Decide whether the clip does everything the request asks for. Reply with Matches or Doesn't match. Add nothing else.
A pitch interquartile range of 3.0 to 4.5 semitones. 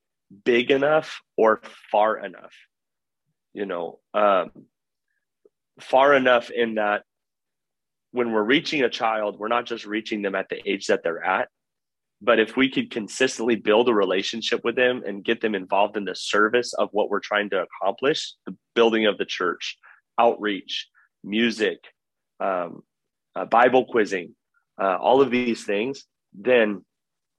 Doesn't match